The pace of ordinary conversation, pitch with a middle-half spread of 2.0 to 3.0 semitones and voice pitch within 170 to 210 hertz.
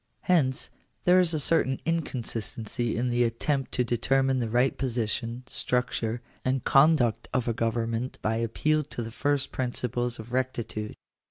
No: average, 155 wpm; narrow, 2.6 semitones; low, 125 Hz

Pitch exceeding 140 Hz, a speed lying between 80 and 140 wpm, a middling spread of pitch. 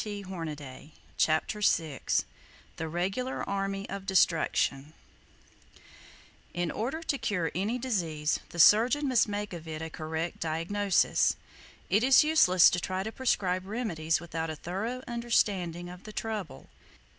Yes: medium, 185 Hz; slow, 135 wpm; average, 5.0 semitones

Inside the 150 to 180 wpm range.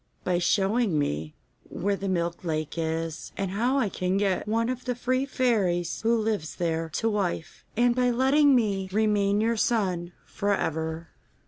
Yes: average, 165 wpm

